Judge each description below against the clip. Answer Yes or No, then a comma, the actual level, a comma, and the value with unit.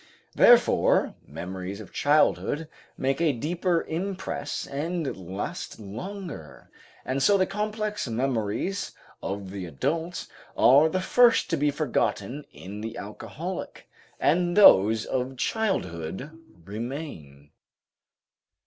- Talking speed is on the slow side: Yes, slow, 105 wpm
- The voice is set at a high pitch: No, medium, 140 Hz